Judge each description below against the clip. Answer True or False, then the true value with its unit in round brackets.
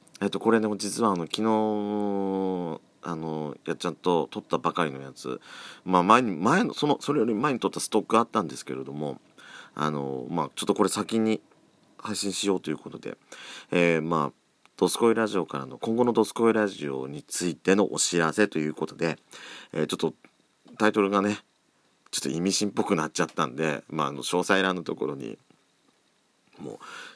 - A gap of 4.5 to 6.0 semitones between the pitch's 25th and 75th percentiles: True (5.2 semitones)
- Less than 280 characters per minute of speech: False (360 characters per minute)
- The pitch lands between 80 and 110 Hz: True (95 Hz)